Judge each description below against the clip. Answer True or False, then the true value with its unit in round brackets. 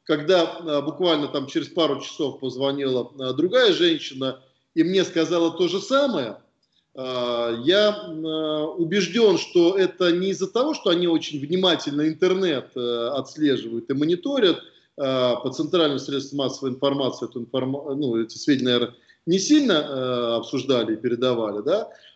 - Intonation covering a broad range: True (5.7 semitones)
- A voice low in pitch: False (150 Hz)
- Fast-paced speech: False (145 wpm)